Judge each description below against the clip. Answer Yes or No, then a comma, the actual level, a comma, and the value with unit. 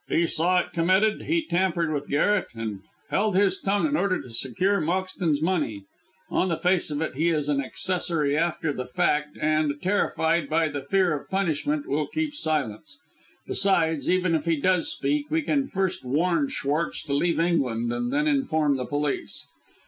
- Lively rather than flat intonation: No, average, 4.4 semitones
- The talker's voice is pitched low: No, medium, 165 Hz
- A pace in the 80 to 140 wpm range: No, average, 180 wpm